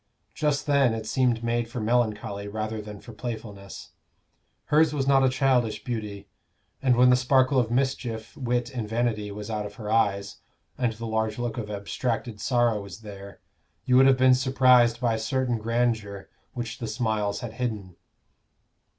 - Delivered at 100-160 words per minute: No, average, 170 wpm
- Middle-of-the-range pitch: No, low, 115 Hz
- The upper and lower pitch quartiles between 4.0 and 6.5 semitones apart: No, average, 2.9 semitones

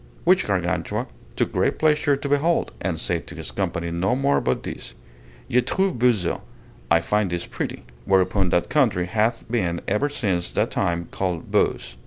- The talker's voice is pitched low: Yes, low, 100 Hz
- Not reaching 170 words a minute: No, average, 175 wpm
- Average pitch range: No, wide, 7.0 semitones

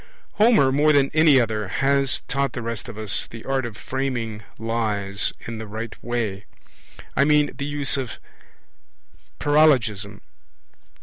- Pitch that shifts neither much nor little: Yes, average, 4.1 semitones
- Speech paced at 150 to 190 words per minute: No, average, 140 wpm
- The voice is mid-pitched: No, low, 120 Hz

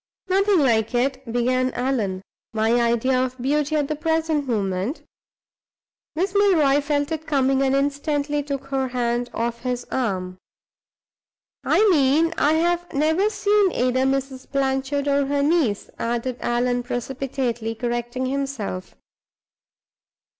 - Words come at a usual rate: No, slow, 130 wpm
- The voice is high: Yes, very high, 270 Hz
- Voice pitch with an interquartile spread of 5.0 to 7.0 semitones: No, average, 3.4 semitones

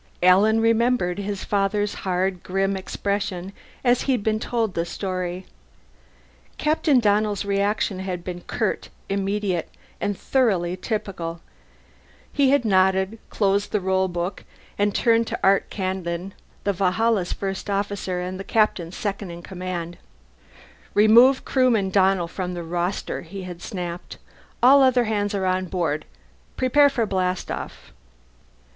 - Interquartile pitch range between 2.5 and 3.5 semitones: Yes, average, 2.8 semitones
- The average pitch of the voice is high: Yes, high, 195 Hz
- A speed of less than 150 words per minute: Yes, slow, 135 wpm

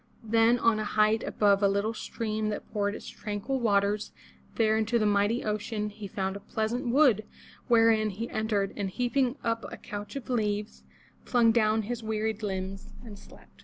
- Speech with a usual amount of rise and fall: No, narrow, 1.9 semitones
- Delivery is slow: No, average, 175 wpm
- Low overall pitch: No, high, 215 Hz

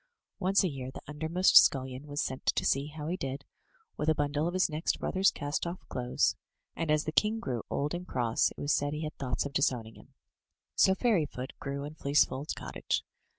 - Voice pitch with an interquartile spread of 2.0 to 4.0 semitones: Yes, average, 3.3 semitones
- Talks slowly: No, fast, 205 wpm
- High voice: No, medium, 150 Hz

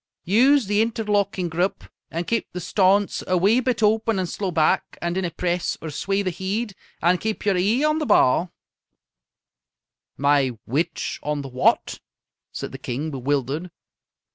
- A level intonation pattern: No, average, 4.7 semitones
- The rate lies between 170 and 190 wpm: No, average, 160 wpm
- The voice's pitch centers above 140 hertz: Yes, medium, 185 Hz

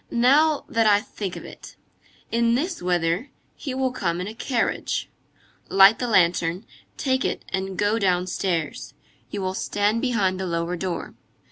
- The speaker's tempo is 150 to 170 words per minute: Yes, average, 155 wpm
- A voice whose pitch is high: Yes, high, 200 Hz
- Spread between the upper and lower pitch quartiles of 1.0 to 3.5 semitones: No, average, 4.6 semitones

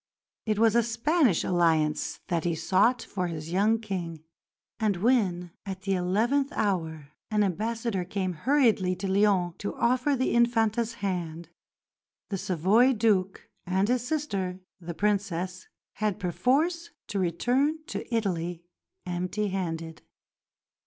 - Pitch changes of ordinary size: Yes, average, 4.7 semitones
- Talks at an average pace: No, slow, 130 wpm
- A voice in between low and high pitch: No, high, 195 Hz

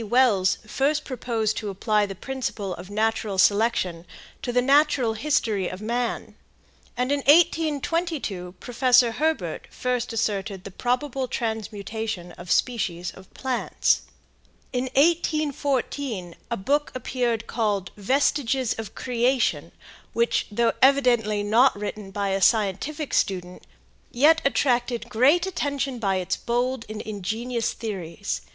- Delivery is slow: Yes, slow, 120 wpm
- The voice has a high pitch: Yes, high, 235 Hz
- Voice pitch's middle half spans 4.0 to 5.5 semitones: Yes, average, 4.5 semitones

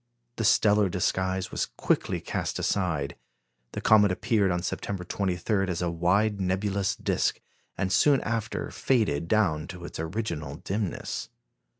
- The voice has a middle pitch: No, very low, 95 Hz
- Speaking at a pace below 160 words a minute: Yes, slow, 135 wpm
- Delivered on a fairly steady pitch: No, average, 3.1 semitones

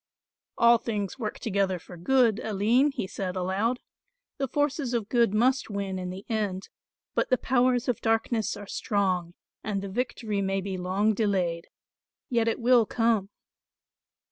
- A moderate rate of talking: Yes, average, 155 wpm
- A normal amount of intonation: Yes, average, 3.6 semitones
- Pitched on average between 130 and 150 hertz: No, high, 215 Hz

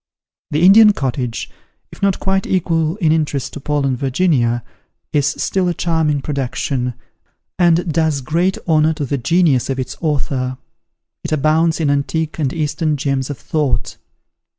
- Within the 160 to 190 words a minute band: No, average, 150 wpm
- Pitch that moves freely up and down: No, average, 3.3 semitones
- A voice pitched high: No, medium, 150 Hz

